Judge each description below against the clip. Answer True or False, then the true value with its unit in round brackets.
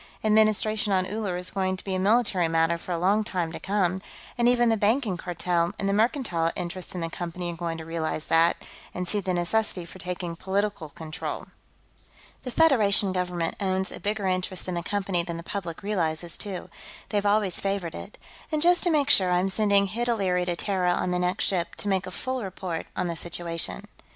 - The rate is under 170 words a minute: False (205 wpm)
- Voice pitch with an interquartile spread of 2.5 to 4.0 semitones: True (3.1 semitones)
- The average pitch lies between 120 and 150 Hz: False (185 Hz)